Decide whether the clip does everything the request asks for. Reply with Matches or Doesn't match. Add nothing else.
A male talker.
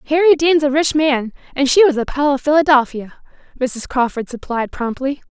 Doesn't match